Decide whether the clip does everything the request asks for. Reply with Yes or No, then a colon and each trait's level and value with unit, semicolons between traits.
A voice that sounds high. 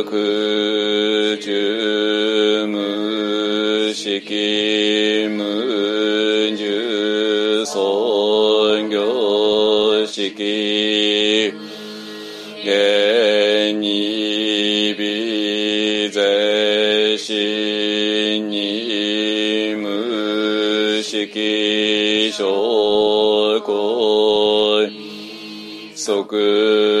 No: low, 105 Hz